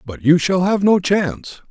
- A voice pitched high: No, medium, 175 Hz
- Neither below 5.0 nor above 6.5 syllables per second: No, 4.8 syllables/s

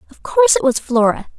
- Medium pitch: No, very high, 315 Hz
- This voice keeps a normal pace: No, fast, 215 wpm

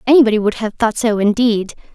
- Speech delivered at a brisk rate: No, average, 185 wpm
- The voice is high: Yes, high, 220 Hz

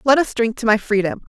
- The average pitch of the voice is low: No, high, 230 Hz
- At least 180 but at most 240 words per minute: No, fast, 265 wpm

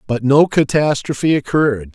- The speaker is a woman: No, male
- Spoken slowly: Yes, slow, 125 wpm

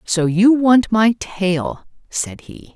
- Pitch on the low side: No, high, 200 Hz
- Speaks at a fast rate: No, average, 155 wpm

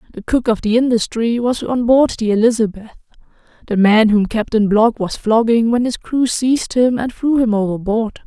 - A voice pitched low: No, high, 230 Hz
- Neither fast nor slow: Yes, average, 190 wpm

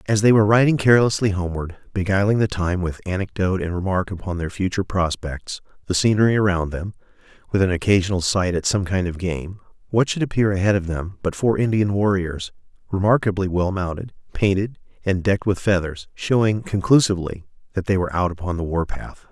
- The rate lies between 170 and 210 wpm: Yes, average, 180 wpm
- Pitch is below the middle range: Yes, very low, 95 Hz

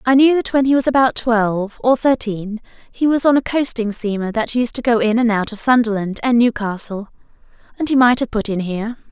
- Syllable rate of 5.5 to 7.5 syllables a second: Yes, 5.6 syllables/s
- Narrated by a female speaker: Yes, female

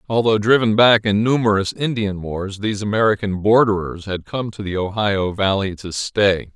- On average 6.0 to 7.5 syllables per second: No, 4.9 syllables/s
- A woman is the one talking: No, male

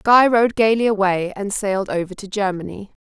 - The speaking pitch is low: No, high, 205 Hz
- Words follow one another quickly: No, average, 175 wpm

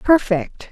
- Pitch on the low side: No, high, 225 Hz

